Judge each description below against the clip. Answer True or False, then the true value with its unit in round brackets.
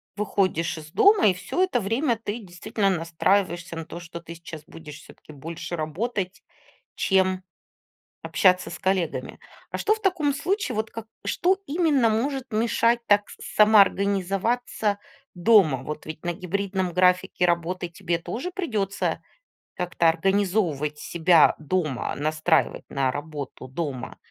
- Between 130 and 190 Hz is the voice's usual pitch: True (185 Hz)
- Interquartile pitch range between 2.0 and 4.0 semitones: False (4.8 semitones)